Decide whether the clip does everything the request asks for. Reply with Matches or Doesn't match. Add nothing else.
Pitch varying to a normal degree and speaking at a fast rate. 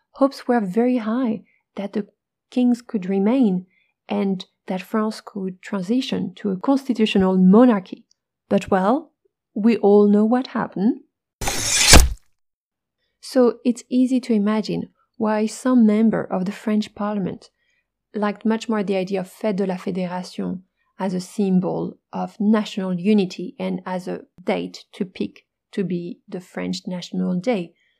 Doesn't match